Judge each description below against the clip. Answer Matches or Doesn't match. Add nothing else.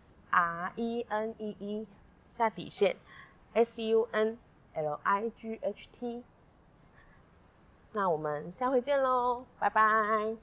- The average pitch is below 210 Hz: Doesn't match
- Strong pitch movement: Doesn't match